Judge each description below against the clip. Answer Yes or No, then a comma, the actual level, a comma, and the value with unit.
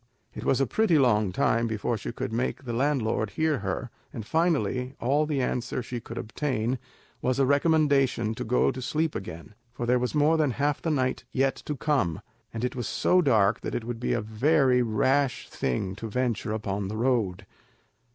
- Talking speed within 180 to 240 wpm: Yes, average, 195 wpm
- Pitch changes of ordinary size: Yes, average, 4.3 semitones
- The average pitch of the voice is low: Yes, low, 125 Hz